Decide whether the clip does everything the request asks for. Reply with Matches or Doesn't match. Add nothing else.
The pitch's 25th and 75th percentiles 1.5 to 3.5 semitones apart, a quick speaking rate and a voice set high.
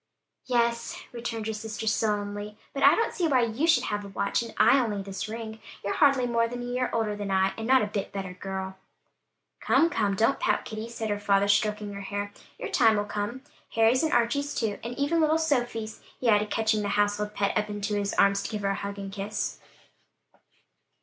Matches